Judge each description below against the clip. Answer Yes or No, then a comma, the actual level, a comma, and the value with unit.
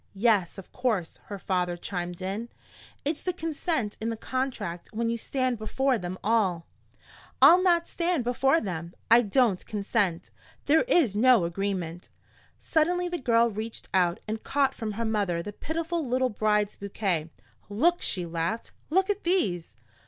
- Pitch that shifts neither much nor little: No, wide, 6.3 semitones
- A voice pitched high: Yes, high, 220 Hz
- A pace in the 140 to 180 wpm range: Yes, average, 155 wpm